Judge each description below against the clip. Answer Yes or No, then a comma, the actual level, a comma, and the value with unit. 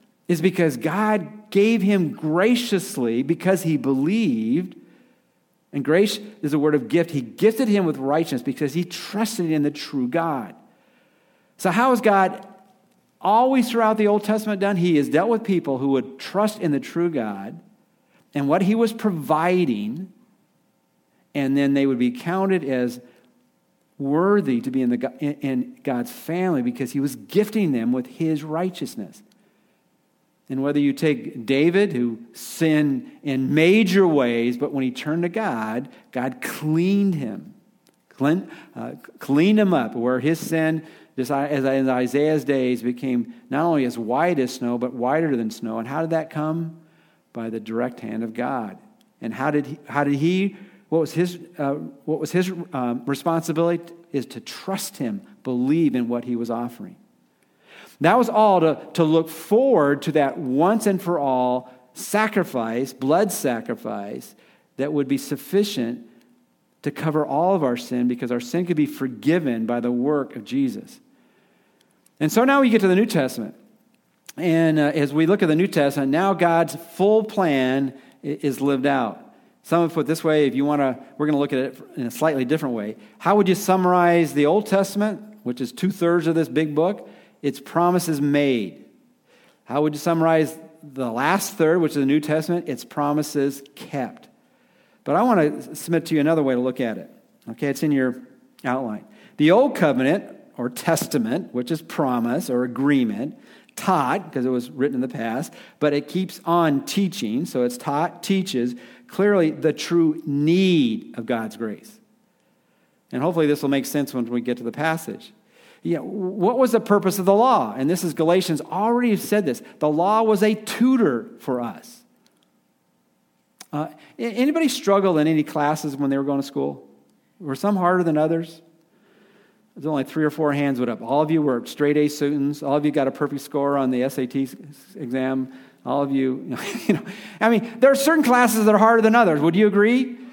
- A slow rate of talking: No, average, 180 wpm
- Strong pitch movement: Yes, wide, 6.4 semitones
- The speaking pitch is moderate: Yes, medium, 155 Hz